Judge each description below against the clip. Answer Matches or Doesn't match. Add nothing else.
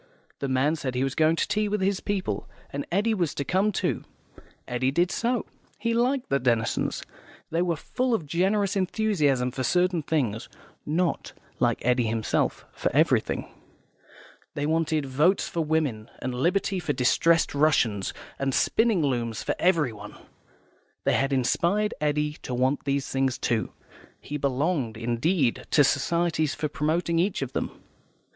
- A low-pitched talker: Doesn't match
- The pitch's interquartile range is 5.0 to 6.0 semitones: Matches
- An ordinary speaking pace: Matches